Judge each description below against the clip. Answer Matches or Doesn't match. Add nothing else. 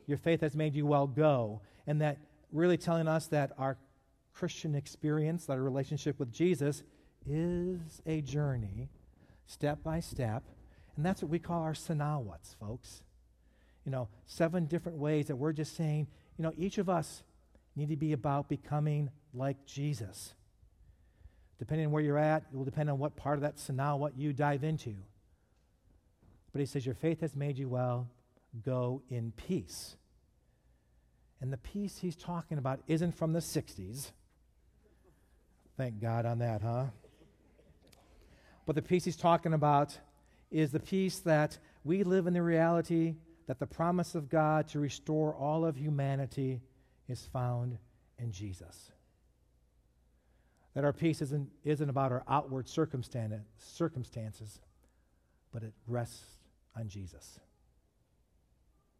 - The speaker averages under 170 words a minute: Matches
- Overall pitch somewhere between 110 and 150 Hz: Matches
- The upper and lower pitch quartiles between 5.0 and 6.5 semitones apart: Matches